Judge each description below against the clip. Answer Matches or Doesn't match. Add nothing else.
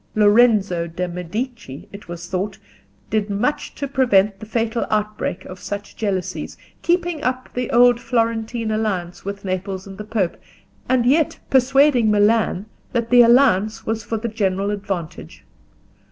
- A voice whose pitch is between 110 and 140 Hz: Doesn't match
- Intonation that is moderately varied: Matches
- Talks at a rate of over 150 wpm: Doesn't match